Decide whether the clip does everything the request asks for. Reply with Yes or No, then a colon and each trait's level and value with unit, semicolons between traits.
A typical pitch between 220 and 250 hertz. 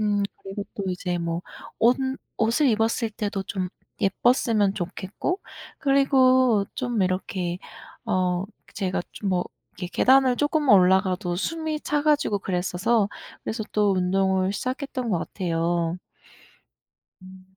No: high, 200 Hz